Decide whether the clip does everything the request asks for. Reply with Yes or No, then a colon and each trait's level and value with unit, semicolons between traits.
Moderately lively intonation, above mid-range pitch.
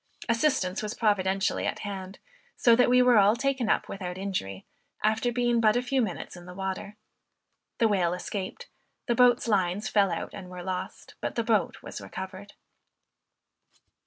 Yes: average, 3.9 semitones; high, 205 Hz